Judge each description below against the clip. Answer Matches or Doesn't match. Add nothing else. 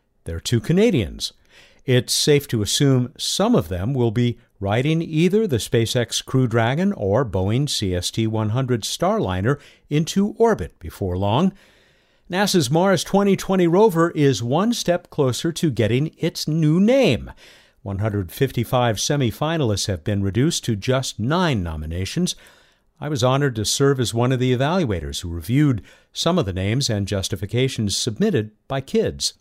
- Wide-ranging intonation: Matches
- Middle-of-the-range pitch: Doesn't match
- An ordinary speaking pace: Matches